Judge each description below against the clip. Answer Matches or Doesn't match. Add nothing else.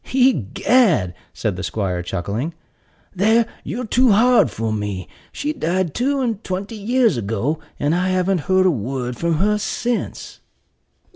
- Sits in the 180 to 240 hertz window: Matches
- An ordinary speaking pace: Matches